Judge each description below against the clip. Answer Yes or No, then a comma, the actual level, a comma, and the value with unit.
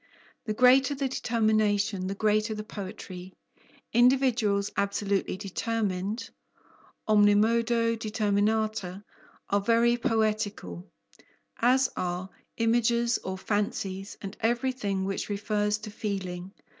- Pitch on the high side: Yes, high, 215 Hz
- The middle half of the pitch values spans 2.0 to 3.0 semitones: Yes, narrow, 2.4 semitones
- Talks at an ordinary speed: No, slow, 95 wpm